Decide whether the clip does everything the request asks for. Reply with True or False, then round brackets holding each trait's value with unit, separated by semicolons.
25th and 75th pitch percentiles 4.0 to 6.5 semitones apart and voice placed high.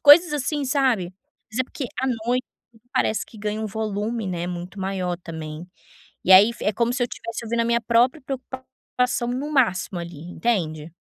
True (5.5 semitones; 225 Hz)